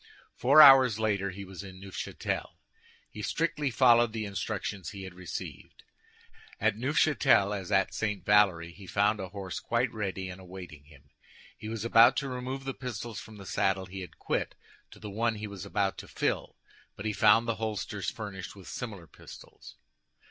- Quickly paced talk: No, average, 175 wpm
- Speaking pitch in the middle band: No, low, 105 Hz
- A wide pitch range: No, average, 3.2 semitones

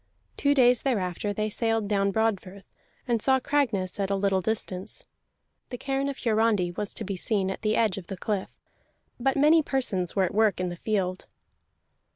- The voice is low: No, high, 210 Hz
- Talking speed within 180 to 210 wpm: Yes, average, 185 wpm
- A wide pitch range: No, average, 4.1 semitones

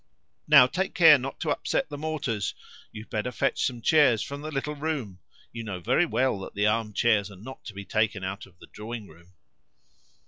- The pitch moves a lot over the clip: Yes, wide, 6.0 semitones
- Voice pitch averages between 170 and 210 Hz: No, low, 115 Hz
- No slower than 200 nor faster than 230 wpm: Yes, fast, 205 wpm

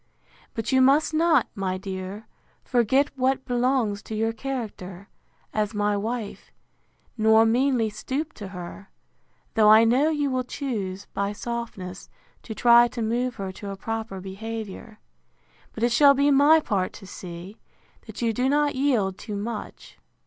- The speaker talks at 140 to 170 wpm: Yes, average, 155 wpm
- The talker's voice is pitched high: Yes, high, 225 Hz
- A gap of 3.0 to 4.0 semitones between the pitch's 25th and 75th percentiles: No, average, 4.4 semitones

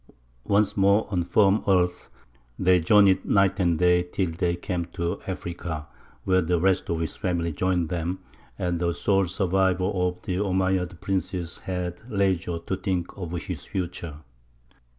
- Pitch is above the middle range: No, very low, 90 Hz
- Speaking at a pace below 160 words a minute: Yes, average, 150 wpm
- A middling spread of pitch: No, narrow, 1.6 semitones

